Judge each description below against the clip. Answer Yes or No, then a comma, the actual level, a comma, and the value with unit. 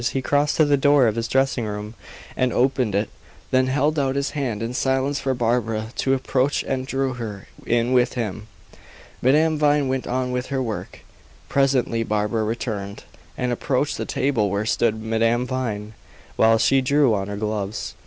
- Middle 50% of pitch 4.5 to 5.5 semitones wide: No, average, 3.4 semitones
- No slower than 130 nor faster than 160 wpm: No, average, 175 wpm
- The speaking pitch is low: Yes, low, 125 Hz